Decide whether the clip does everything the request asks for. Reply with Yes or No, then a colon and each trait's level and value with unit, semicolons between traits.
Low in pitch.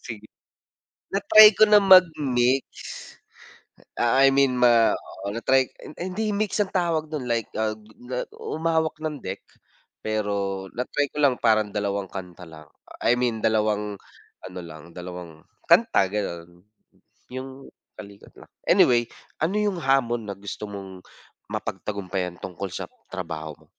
Yes: low, 110 Hz